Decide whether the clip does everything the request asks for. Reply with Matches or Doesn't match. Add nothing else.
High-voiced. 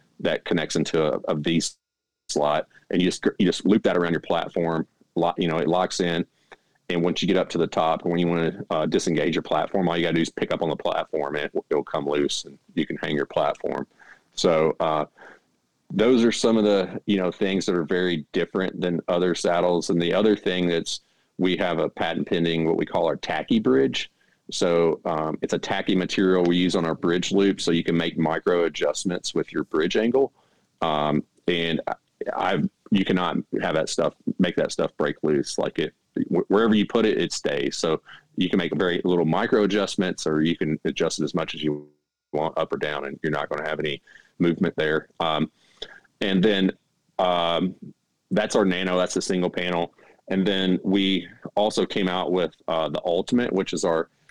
Doesn't match